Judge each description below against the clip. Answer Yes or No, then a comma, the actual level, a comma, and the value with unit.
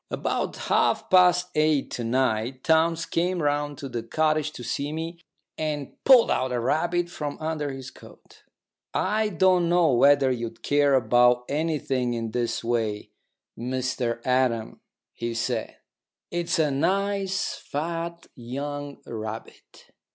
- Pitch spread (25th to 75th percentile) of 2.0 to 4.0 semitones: No, average, 5.2 semitones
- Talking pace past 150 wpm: No, slow, 135 wpm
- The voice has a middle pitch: Yes, medium, 145 Hz